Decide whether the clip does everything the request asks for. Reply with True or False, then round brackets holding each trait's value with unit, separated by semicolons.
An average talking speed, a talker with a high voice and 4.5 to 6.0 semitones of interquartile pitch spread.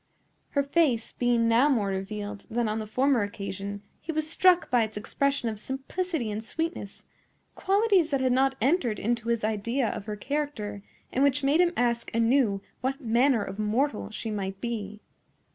True (170 wpm; 235 Hz; 4.9 semitones)